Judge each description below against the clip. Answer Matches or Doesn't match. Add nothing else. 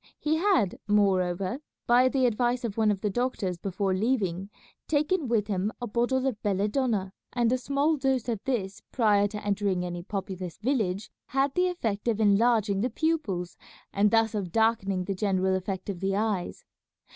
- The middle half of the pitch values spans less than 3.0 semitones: Doesn't match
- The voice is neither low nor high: Doesn't match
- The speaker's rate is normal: Matches